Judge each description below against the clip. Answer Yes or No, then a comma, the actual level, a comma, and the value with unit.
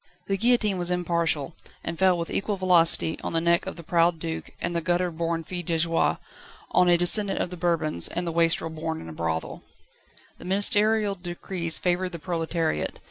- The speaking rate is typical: Yes, average, 190 wpm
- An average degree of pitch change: No, narrow, 1.7 semitones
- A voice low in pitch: No, medium, 170 Hz